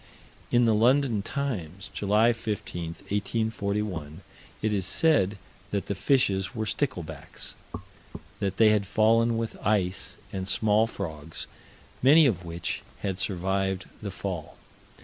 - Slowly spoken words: Yes, slow, 125 wpm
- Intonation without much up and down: No, average, 3.3 semitones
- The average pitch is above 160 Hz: No, low, 100 Hz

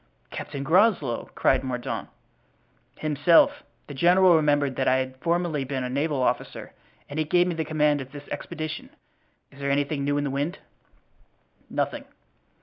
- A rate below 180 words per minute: Yes, average, 155 wpm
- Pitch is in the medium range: Yes, medium, 145 Hz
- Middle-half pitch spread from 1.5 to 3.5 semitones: Yes, average, 2.9 semitones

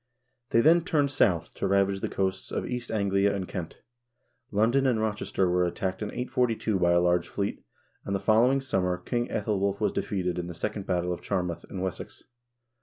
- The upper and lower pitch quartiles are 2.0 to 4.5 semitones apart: Yes, average, 3.9 semitones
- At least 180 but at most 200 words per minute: Yes, average, 195 wpm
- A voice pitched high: No, low, 100 Hz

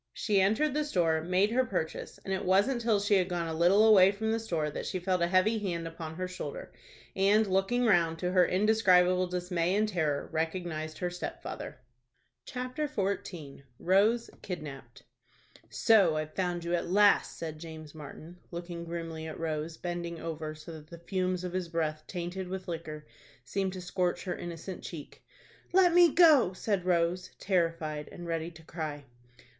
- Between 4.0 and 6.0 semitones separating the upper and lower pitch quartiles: No, average, 3.1 semitones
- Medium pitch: Yes, medium, 180 Hz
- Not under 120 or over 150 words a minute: No, average, 175 wpm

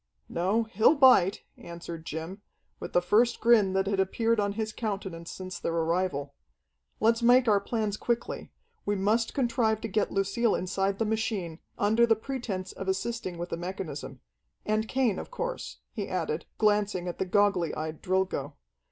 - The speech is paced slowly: No, average, 165 wpm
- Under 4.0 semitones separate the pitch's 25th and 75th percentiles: Yes, average, 3.6 semitones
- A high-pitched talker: Yes, high, 200 Hz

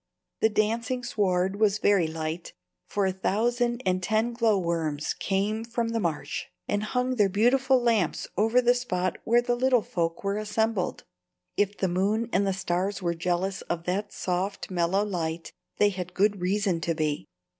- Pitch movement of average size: Yes, average, 3.9 semitones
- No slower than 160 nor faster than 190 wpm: Yes, average, 165 wpm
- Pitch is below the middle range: No, high, 200 Hz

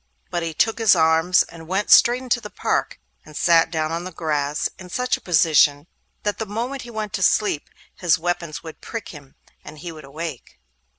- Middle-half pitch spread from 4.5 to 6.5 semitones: Yes, average, 4.9 semitones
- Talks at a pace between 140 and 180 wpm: No, average, 195 wpm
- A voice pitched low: No, medium, 170 Hz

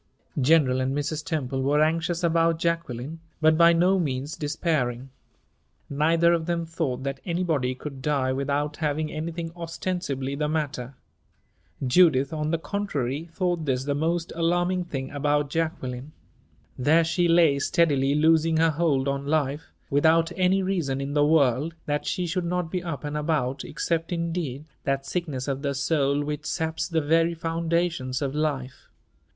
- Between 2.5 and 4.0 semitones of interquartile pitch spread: Yes, average, 3.2 semitones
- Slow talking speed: No, average, 155 wpm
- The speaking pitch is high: No, medium, 155 Hz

